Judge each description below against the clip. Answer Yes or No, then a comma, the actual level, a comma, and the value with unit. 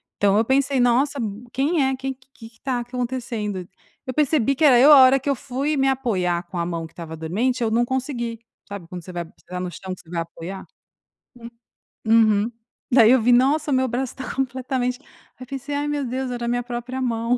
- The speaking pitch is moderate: No, high, 245 Hz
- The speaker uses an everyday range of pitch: Yes, average, 4.1 semitones